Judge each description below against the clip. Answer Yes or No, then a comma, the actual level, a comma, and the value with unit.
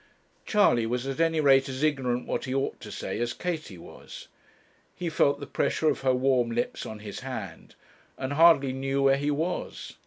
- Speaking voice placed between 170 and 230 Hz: No, low, 135 Hz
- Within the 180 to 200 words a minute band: Yes, average, 190 wpm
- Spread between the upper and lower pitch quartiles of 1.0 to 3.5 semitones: Yes, average, 3.1 semitones